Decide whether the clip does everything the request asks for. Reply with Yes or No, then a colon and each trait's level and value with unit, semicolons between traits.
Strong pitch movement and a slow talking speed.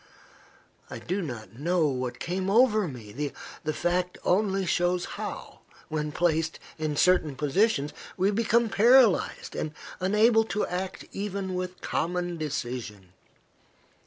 No: average, 4.7 semitones; slow, 125 wpm